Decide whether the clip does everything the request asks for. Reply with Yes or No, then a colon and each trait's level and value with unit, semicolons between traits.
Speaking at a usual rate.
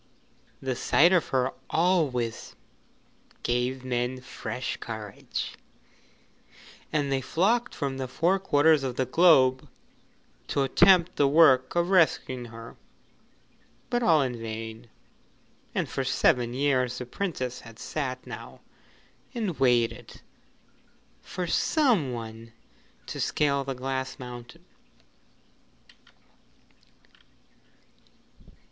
No: slow, 100 wpm